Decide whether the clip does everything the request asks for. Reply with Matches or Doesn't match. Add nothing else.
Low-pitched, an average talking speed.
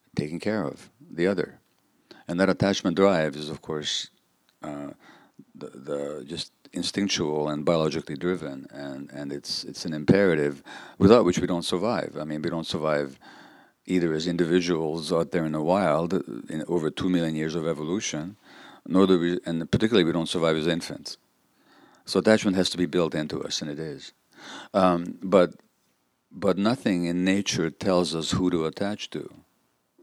Matches